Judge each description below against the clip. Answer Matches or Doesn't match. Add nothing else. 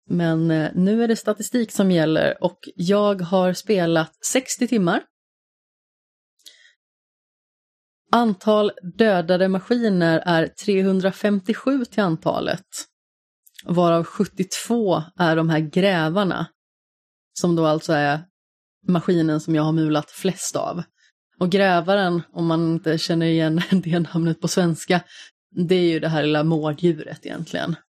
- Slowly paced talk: Matches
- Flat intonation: Doesn't match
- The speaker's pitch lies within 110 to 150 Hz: Doesn't match